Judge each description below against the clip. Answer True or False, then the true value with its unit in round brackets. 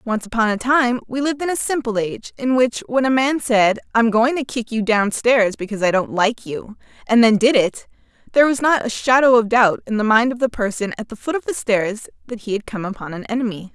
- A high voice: True (230 Hz)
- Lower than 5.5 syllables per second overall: False (5.8 syllables/s)